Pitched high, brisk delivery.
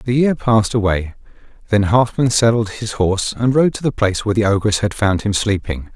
No: low, 110 Hz; fast, 210 wpm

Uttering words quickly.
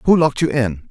Yes: fast, 265 wpm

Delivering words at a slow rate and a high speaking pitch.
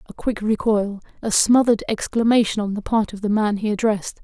No: average, 200 wpm; high, 215 Hz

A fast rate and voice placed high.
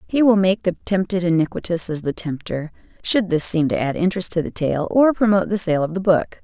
No: fast, 235 wpm; medium, 180 Hz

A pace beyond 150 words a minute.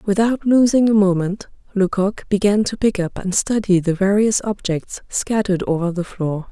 Yes: average, 165 wpm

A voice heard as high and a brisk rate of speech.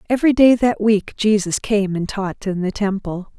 No: high, 205 Hz; average, 195 wpm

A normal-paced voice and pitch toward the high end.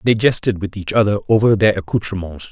No: average, 190 wpm; low, 100 Hz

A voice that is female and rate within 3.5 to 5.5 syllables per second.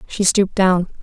Yes: female; 5.3 syllables/s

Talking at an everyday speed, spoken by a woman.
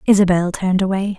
Yes: average, 150 wpm; female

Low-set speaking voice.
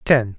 Yes: low, 120 Hz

